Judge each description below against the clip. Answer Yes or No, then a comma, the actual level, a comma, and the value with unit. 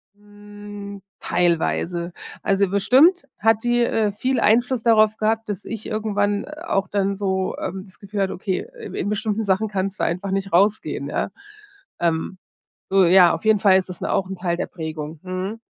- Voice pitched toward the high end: Yes, high, 200 Hz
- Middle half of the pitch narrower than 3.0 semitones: Yes, narrow, 2.4 semitones